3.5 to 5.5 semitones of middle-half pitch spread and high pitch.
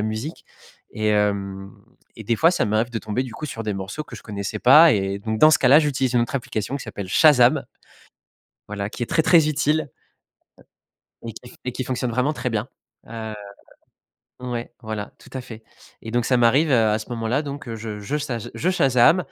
No: average, 4.1 semitones; low, 120 Hz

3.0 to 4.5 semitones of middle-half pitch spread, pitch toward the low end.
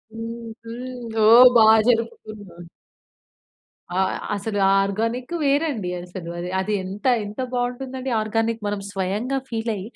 No: average, 3.3 semitones; high, 225 Hz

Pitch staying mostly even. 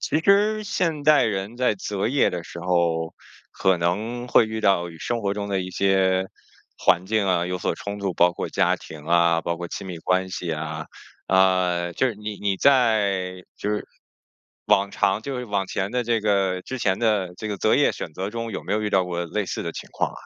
No: average, 3.4 semitones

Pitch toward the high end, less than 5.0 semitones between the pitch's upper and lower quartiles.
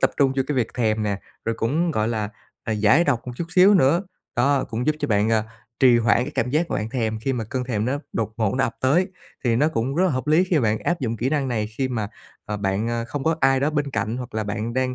No: low, 125 Hz; average, 4.4 semitones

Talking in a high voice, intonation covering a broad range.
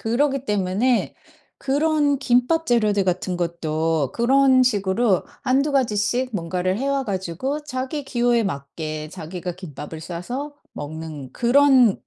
Yes: high, 220 Hz; wide, 7.3 semitones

